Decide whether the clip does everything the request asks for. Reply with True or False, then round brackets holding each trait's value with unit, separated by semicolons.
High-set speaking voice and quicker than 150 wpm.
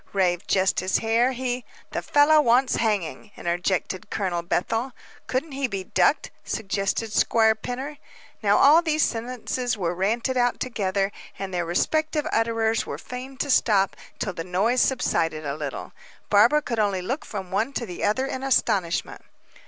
True (225 Hz; 160 wpm)